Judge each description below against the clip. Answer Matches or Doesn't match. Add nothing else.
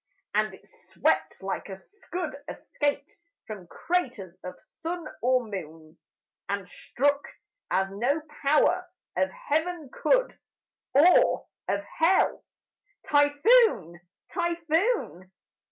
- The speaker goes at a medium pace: Doesn't match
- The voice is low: Doesn't match